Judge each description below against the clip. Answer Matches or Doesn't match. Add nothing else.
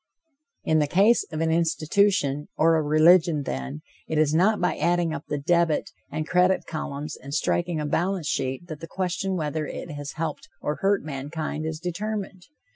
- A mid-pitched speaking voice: Matches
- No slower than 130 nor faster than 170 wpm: Doesn't match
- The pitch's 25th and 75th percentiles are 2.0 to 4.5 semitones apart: Matches